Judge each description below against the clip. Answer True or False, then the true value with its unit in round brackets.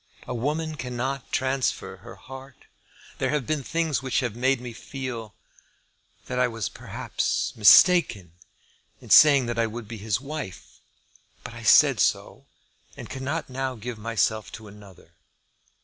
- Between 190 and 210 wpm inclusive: False (150 wpm)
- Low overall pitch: True (125 Hz)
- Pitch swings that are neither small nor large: True (3.3 semitones)